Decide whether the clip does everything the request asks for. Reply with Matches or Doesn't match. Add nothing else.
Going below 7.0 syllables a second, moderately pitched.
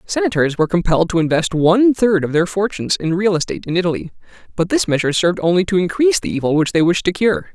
Doesn't match